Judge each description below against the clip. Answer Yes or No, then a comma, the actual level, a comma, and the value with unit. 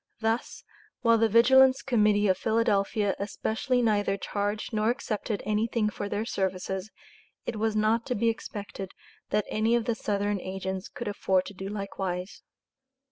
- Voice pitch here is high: Yes, high, 210 Hz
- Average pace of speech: Yes, average, 150 wpm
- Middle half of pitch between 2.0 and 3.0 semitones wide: Yes, narrow, 2.4 semitones